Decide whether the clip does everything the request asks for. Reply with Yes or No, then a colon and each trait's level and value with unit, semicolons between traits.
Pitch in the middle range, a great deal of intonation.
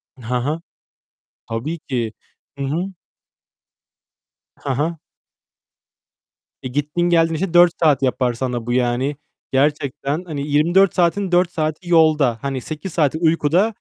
No: medium, 150 Hz; average, 4.3 semitones